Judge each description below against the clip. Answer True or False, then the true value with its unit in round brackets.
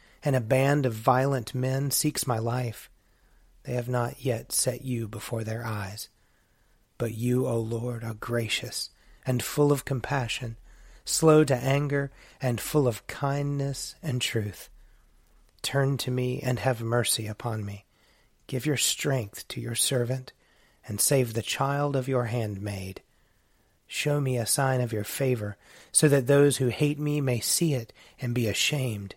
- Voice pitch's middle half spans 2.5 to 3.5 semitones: True (3.1 semitones)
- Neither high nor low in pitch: False (125 Hz)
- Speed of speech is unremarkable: True (160 wpm)